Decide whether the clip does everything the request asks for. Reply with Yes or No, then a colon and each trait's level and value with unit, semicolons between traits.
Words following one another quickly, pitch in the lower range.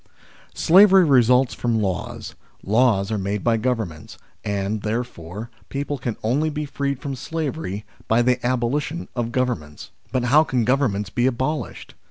No: average, 150 wpm; low, 120 Hz